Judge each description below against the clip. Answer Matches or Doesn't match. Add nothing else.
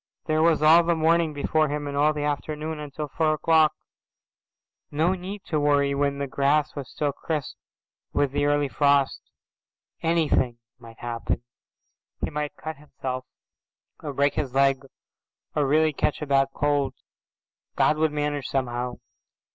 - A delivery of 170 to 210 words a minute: Doesn't match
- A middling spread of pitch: Doesn't match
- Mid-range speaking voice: Matches